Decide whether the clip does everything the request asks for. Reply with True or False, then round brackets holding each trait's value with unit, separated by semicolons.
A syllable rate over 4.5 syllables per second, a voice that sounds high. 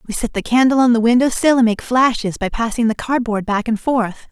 True (5.6 syllables/s; 235 Hz)